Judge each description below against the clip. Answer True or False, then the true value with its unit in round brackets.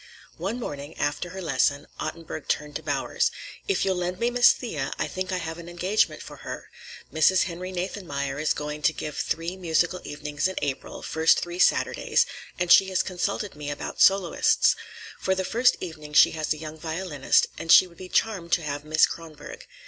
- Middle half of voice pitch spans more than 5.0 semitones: False (3.8 semitones)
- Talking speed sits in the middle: True (190 wpm)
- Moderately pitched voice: True (165 Hz)